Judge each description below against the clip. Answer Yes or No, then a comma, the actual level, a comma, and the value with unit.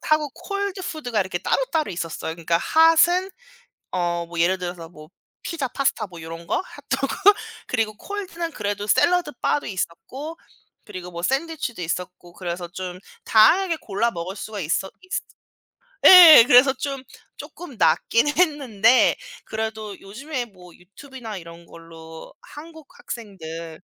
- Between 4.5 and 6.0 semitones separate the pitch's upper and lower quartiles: No, wide, 9.0 semitones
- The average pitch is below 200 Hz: No, high, 215 Hz